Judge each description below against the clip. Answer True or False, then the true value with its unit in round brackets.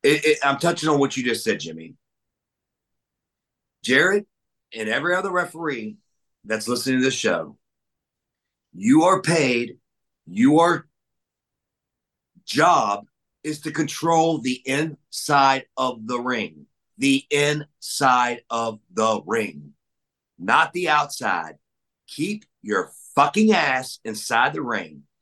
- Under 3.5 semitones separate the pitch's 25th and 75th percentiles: False (4.9 semitones)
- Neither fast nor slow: False (115 wpm)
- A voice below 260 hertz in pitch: True (140 Hz)